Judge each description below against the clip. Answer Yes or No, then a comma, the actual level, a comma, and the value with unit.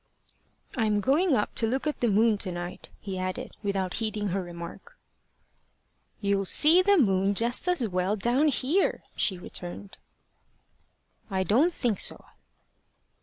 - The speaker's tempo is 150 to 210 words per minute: No, average, 140 wpm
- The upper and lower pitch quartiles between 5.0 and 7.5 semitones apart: Yes, wide, 5.6 semitones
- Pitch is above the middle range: Yes, high, 210 Hz